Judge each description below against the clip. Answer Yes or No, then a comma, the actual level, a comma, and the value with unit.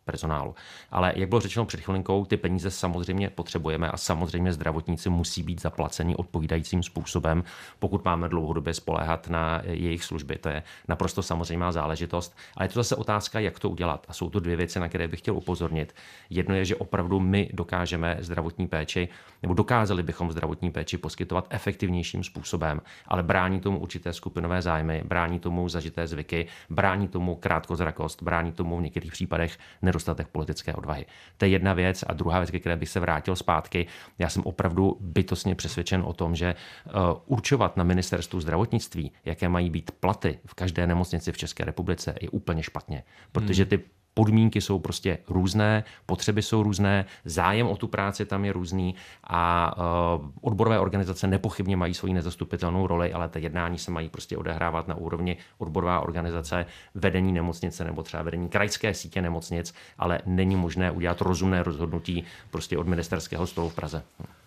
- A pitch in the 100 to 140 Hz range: No, very low, 90 Hz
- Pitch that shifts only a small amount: Yes, narrow, 2.1 semitones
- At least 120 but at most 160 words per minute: No, fast, 170 wpm